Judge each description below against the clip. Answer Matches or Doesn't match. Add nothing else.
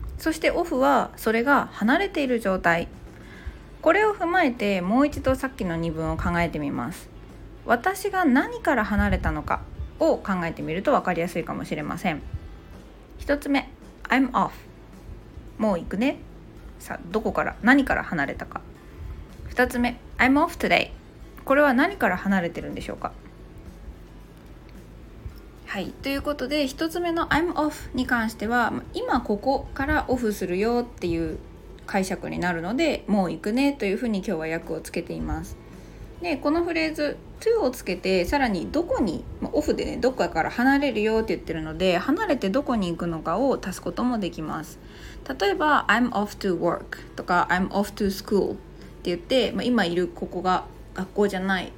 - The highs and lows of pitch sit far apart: Matches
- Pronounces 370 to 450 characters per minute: Doesn't match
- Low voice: Doesn't match